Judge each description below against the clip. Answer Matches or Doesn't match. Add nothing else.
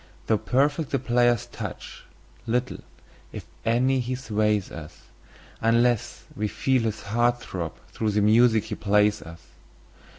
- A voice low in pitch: Matches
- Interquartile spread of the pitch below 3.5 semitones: Matches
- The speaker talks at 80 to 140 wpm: Matches